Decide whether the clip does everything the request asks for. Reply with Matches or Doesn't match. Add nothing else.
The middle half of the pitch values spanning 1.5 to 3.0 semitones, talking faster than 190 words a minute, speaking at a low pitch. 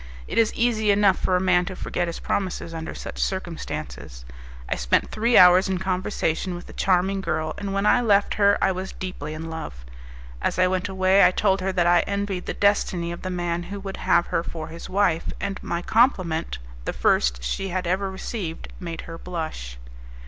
Doesn't match